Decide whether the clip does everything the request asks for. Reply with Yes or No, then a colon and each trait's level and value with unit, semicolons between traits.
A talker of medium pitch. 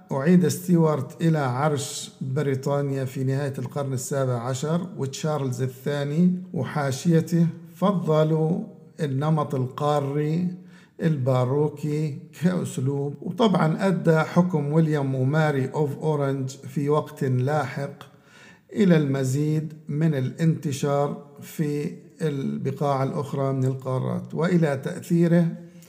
Yes: medium, 150 Hz